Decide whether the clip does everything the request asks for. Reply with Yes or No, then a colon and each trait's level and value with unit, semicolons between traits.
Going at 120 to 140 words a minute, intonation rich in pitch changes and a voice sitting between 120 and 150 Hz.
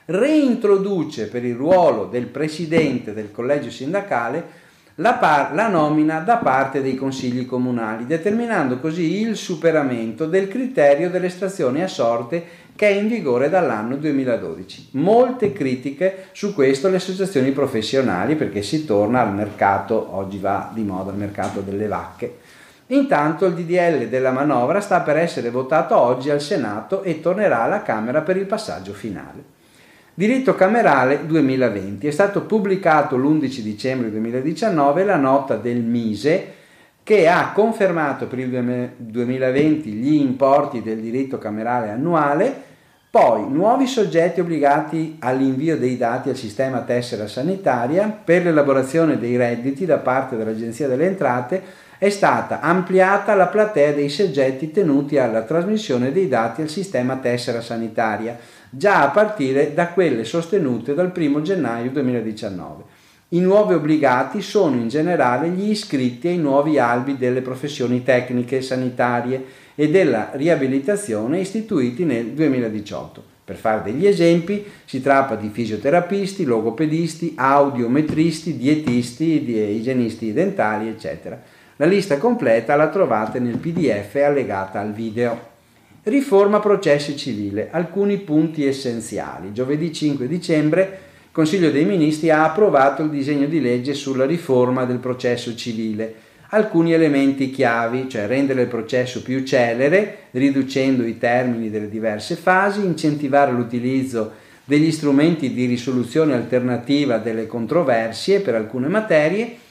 Yes: average, 130 wpm; wide, 5.9 semitones; medium, 140 Hz